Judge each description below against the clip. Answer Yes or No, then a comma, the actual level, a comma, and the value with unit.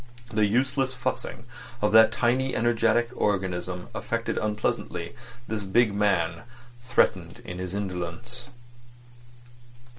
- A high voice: No, low, 105 Hz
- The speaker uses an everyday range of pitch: Yes, average, 4.2 semitones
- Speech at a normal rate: No, slow, 100 wpm